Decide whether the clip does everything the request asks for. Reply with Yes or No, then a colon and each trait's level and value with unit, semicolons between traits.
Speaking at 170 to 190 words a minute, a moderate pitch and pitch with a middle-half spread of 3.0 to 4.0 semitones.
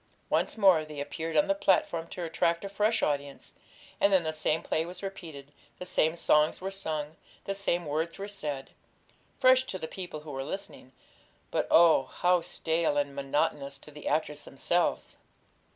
Yes: average, 175 wpm; medium, 160 Hz; average, 3.7 semitones